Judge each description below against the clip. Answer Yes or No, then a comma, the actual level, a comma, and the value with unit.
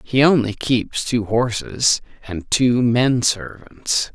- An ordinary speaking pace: No, slow, 130 wpm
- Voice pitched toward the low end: Yes, low, 115 Hz